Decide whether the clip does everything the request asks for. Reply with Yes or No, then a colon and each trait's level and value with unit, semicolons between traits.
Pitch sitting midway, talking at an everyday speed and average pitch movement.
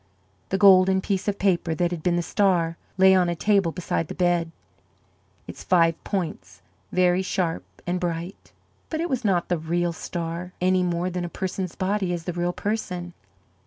No: medium, 180 Hz; average, 180 wpm; narrow, 1.7 semitones